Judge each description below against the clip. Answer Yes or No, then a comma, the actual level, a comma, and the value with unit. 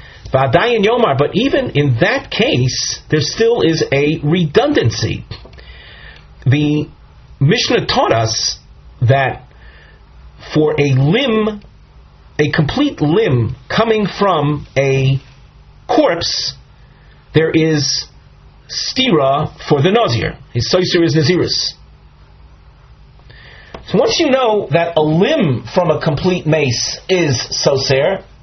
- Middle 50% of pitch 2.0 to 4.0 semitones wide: No, average, 4.6 semitones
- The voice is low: No, medium, 145 Hz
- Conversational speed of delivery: No, slow, 100 wpm